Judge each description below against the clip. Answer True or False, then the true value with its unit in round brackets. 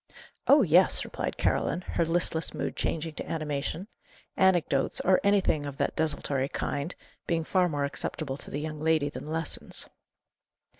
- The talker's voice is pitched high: False (160 Hz)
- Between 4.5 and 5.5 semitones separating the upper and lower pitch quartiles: False (3.2 semitones)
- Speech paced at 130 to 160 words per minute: True (150 wpm)